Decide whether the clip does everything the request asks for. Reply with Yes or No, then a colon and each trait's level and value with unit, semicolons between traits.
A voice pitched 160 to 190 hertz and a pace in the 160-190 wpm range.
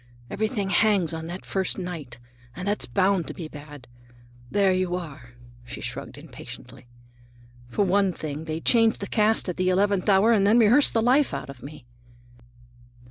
Yes: medium, 185 Hz; average, 170 wpm